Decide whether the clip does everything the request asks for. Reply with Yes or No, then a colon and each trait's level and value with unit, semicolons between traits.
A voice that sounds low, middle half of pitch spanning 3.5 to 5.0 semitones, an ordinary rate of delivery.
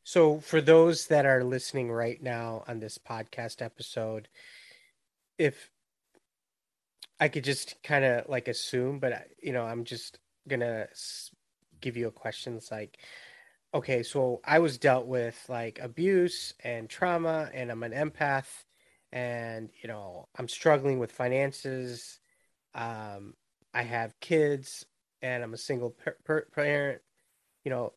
Yes: low, 125 Hz; average, 3.9 semitones; average, 145 wpm